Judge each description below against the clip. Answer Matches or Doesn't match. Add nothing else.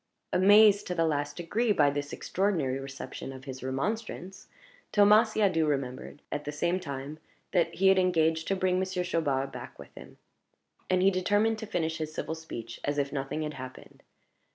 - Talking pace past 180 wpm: Doesn't match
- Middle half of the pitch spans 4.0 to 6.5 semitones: Matches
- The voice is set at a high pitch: Doesn't match